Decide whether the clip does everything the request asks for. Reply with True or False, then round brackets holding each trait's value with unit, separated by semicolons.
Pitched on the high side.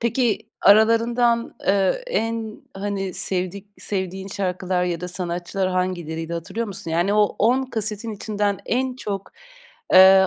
True (200 Hz)